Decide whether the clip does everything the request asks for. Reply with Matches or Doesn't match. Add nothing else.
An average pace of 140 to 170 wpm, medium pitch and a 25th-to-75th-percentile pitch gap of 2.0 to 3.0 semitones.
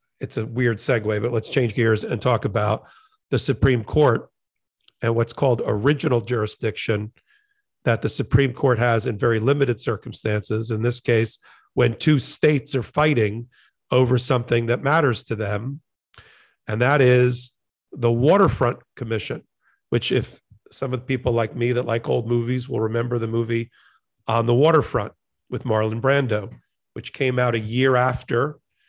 Doesn't match